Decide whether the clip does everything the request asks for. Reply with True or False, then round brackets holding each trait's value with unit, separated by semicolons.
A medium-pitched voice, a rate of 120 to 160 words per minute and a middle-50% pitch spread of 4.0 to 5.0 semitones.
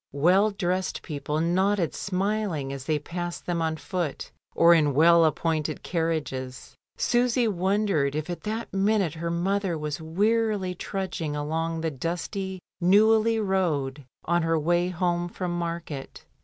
False (175 Hz; 140 wpm; 3.4 semitones)